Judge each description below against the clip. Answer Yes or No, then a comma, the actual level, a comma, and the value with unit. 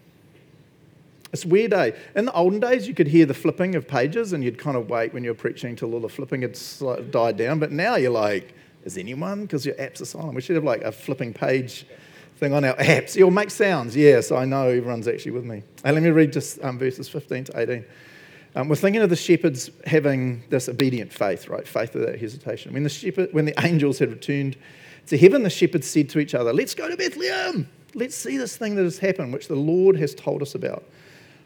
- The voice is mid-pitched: Yes, medium, 150 Hz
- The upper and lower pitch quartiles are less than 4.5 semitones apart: No, average, 4.9 semitones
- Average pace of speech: No, fast, 235 wpm